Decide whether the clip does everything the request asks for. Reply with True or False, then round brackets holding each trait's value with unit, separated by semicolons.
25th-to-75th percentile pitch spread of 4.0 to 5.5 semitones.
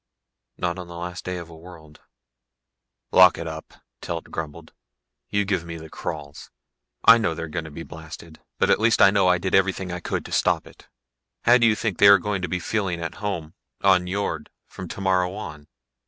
False (3.0 semitones)